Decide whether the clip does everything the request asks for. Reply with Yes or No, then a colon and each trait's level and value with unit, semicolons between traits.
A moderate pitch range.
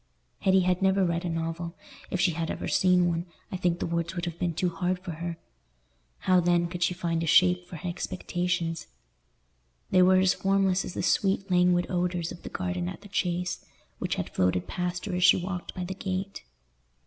No: narrow, 1.4 semitones